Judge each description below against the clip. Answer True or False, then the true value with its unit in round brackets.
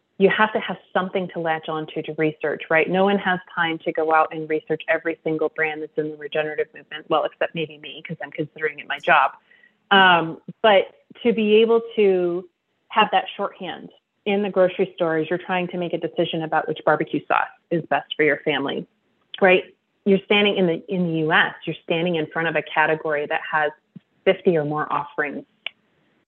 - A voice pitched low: False (165 Hz)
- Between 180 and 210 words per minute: True (200 wpm)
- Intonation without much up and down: False (3.5 semitones)